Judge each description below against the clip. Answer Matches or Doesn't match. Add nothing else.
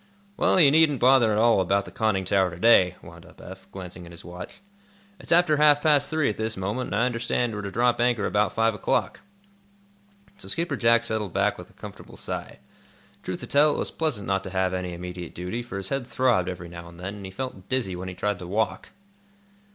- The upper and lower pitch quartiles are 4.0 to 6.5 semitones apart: Matches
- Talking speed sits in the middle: Doesn't match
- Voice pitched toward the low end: Matches